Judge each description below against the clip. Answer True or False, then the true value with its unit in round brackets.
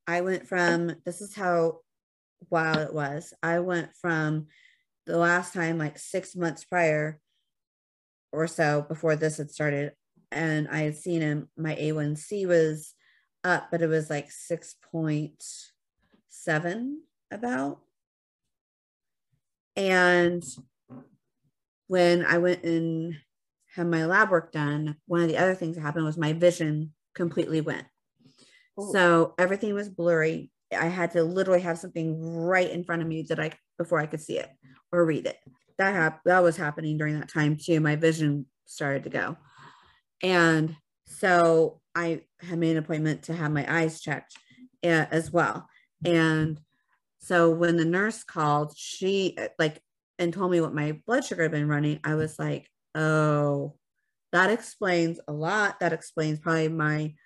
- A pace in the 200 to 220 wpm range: False (155 wpm)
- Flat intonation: True (2.3 semitones)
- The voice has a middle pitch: True (165 Hz)